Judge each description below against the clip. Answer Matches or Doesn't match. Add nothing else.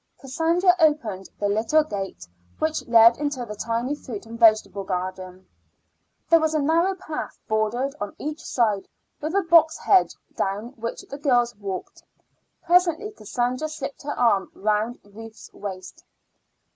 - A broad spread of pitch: Matches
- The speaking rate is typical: Matches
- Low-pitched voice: Doesn't match